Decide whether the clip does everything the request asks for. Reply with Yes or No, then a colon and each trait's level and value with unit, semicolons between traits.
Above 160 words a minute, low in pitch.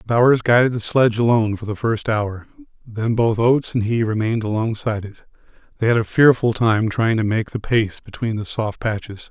Yes: average, 200 wpm; low, 110 Hz